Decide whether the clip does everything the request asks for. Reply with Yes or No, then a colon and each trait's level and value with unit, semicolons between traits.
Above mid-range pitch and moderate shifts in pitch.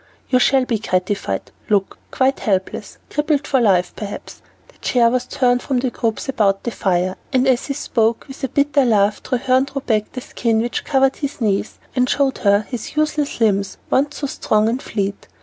Yes: high, 245 Hz; average, 4.4 semitones